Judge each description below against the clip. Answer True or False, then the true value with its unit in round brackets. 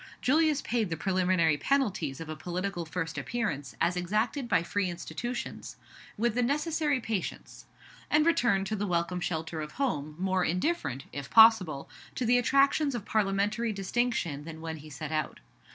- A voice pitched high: True (195 Hz)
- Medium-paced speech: True (160 wpm)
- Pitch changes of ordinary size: False (6.7 semitones)